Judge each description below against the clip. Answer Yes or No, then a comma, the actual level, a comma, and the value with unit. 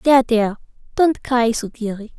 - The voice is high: Yes, high, 235 Hz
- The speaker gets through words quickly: No, slow, 110 wpm